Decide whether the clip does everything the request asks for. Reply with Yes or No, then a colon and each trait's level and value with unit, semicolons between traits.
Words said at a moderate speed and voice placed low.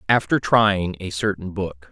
Yes: average, 155 wpm; very low, 95 Hz